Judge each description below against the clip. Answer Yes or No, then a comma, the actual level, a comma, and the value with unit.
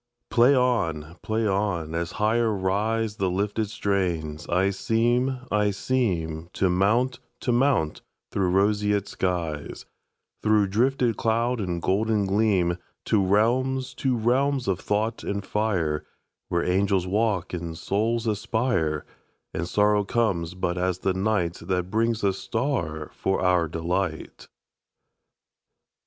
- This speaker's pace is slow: Yes, slow, 110 wpm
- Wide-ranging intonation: No, average, 4.0 semitones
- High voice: No, low, 100 Hz